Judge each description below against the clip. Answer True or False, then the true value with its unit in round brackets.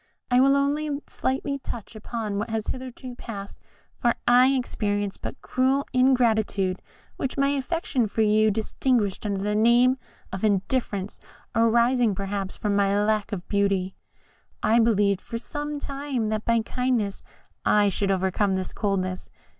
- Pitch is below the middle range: False (220 Hz)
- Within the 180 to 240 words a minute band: False (145 wpm)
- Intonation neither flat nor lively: True (4.1 semitones)